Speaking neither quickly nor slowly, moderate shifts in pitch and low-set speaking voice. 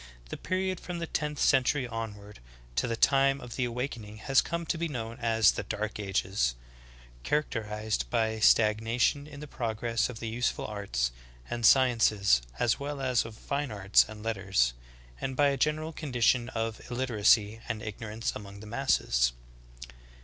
Yes: average, 165 wpm; average, 4.1 semitones; low, 115 Hz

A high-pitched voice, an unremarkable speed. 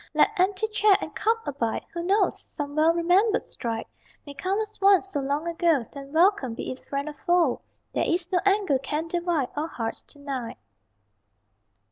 Yes: very high, 330 Hz; average, 180 wpm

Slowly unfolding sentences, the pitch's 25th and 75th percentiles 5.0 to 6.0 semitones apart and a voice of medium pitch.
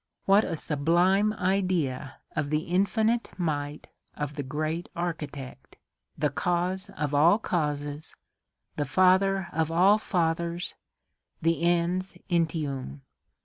No: slow, 110 wpm; average, 3.9 semitones; medium, 170 Hz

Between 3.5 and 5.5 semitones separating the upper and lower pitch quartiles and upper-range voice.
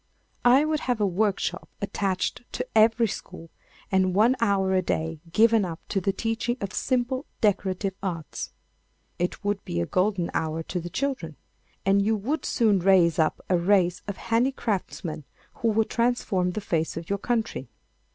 Yes: average, 4.1 semitones; high, 200 Hz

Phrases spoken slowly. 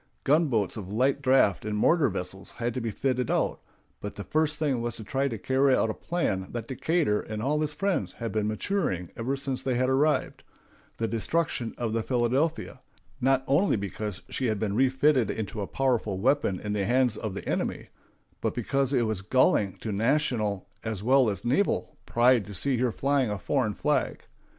No: average, 190 wpm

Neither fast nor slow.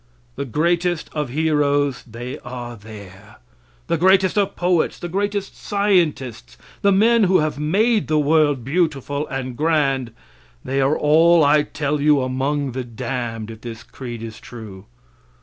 Yes: average, 150 wpm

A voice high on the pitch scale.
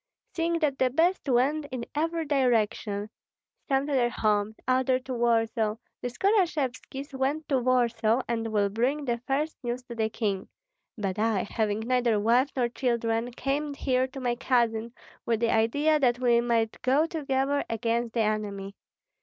Yes: high, 245 Hz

